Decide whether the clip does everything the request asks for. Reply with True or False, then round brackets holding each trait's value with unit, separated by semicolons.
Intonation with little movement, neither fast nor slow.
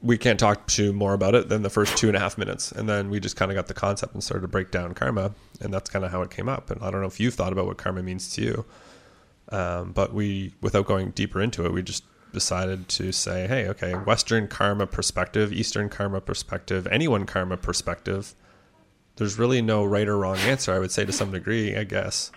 False (2.3 semitones; 245 wpm)